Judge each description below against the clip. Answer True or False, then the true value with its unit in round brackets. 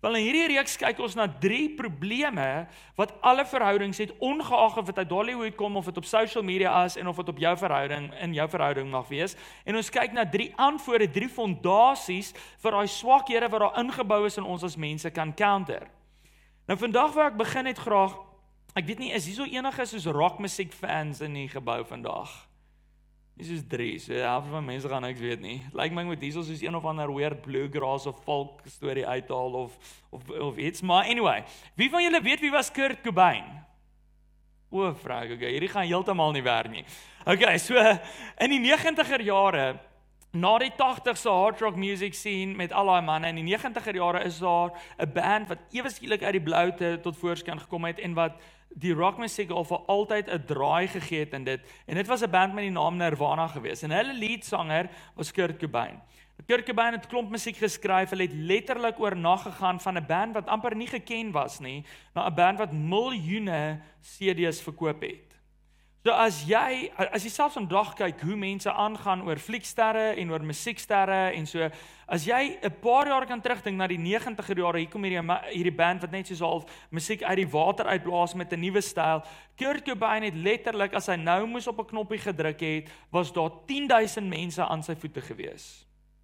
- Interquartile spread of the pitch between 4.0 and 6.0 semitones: True (5.2 semitones)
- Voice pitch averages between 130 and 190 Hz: True (185 Hz)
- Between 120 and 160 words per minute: False (195 wpm)